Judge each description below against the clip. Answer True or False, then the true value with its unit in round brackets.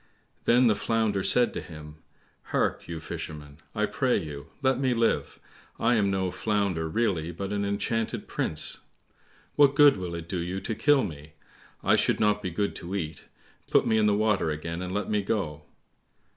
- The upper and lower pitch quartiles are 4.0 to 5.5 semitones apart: True (5.0 semitones)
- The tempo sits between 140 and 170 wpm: False (185 wpm)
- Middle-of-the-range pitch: False (100 Hz)